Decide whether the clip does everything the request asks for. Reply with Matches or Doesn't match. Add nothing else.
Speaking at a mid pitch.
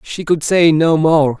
Matches